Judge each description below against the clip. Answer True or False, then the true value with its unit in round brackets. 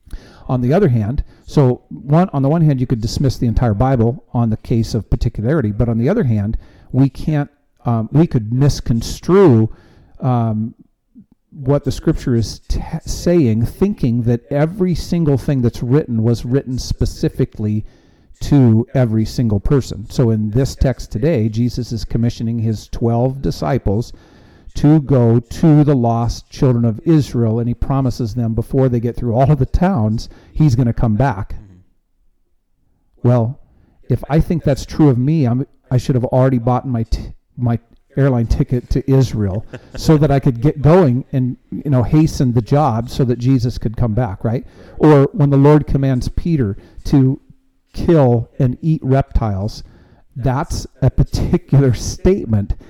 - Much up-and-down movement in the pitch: False (3.4 semitones)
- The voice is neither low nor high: False (125 Hz)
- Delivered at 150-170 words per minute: True (165 wpm)